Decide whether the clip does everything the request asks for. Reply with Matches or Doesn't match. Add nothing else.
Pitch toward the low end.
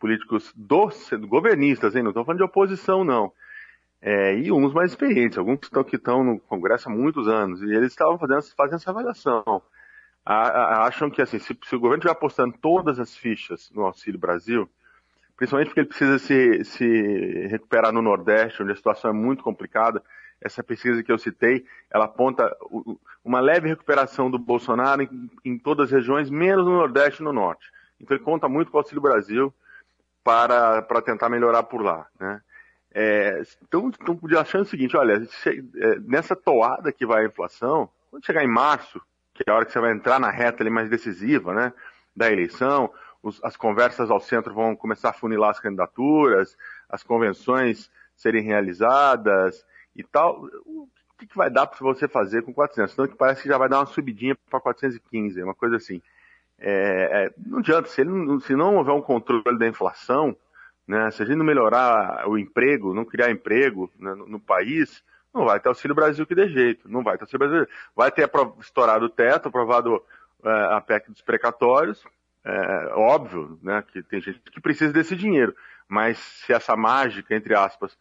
Matches